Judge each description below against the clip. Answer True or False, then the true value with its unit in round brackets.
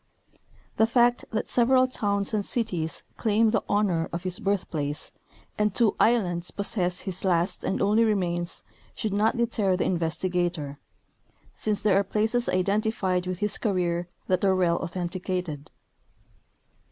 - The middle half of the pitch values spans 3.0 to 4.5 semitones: True (3.5 semitones)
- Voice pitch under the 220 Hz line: True (190 Hz)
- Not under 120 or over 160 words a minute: True (145 wpm)